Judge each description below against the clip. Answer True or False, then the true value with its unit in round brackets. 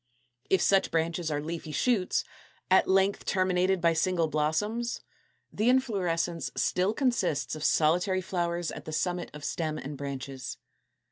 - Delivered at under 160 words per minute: True (140 wpm)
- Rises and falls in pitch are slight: False (3.4 semitones)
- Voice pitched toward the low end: False (175 Hz)